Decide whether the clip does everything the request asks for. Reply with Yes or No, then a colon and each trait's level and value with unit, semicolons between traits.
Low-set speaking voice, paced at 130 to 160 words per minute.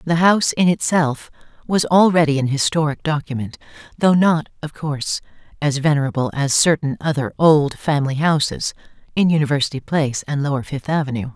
No: medium, 150 Hz; average, 150 wpm